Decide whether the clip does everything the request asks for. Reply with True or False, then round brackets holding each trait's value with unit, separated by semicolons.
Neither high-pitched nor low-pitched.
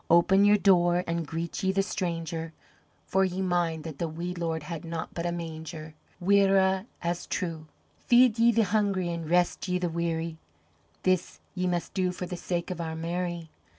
True (175 Hz)